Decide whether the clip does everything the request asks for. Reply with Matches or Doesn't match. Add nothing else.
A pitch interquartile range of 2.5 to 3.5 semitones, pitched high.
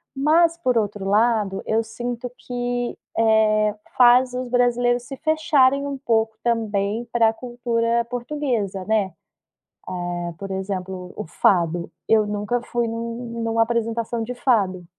Matches